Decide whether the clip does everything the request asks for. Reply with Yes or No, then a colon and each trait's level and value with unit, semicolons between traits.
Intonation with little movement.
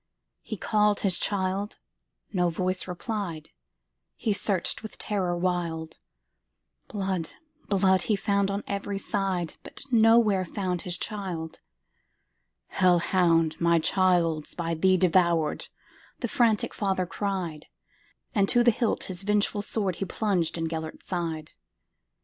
No: average, 3.3 semitones